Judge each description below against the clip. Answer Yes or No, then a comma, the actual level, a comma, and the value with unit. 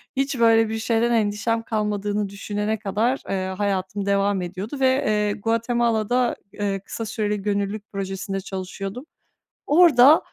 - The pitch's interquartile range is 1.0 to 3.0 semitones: Yes, narrow, 2.5 semitones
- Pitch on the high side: Yes, high, 210 Hz